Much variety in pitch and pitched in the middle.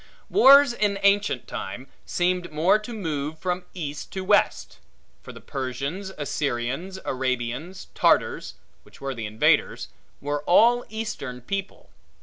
Yes: wide, 6.8 semitones; medium, 165 Hz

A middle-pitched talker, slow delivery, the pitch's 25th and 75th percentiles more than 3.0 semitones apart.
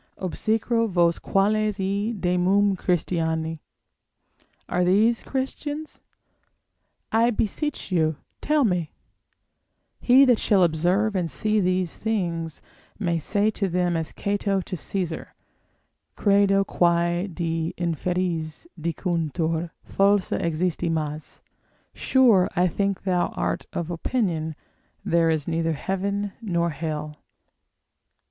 Yes: medium, 180 Hz; slow, 105 wpm; average, 3.5 semitones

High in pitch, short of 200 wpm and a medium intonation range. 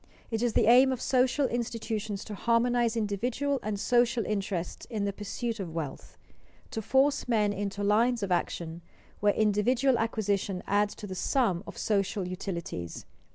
Yes: high, 215 Hz; average, 155 wpm; average, 3.3 semitones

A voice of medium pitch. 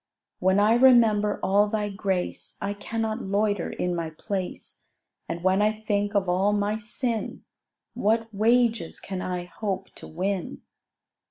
No: high, 205 Hz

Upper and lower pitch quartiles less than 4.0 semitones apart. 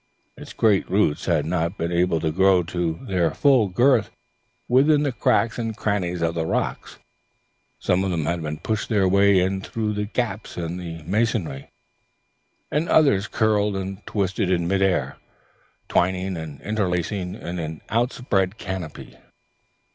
Yes: average, 3.6 semitones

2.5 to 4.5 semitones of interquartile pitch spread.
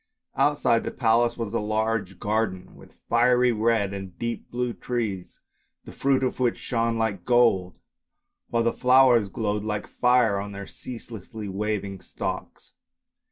Yes: average, 3.0 semitones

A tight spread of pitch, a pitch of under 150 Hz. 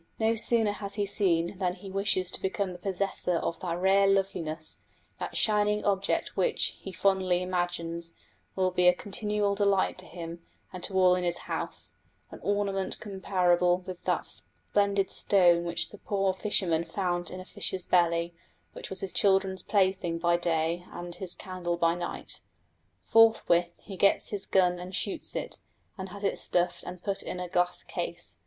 No: narrow, 2.1 semitones; medium, 185 Hz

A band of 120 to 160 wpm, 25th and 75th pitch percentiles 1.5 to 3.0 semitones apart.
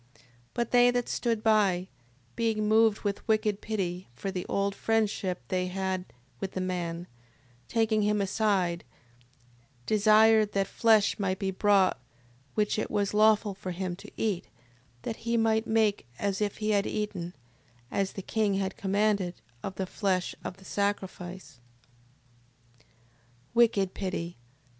Yes: average, 145 wpm; narrow, 2.4 semitones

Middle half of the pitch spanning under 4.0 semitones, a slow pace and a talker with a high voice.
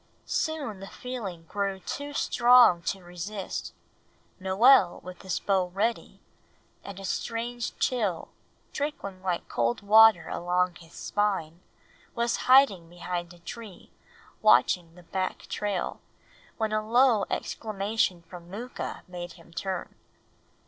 No: average, 4.3 semitones; slow, 120 wpm; high, 195 Hz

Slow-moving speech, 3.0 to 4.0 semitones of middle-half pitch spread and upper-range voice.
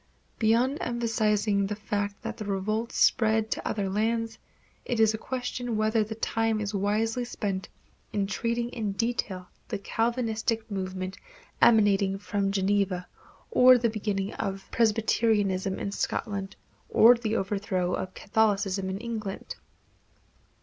No: slow, 130 wpm; narrow, 2.5 semitones; high, 215 Hz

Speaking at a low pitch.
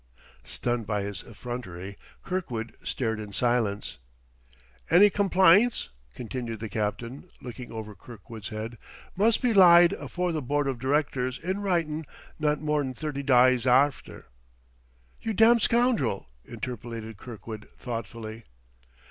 Yes: low, 125 Hz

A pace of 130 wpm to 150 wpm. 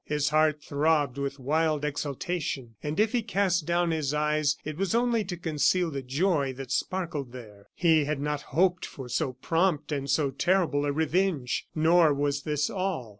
No: average, 175 wpm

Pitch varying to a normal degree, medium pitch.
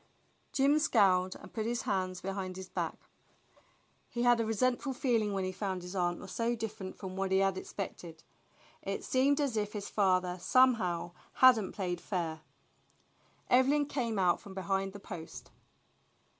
No: average, 4.5 semitones; high, 195 Hz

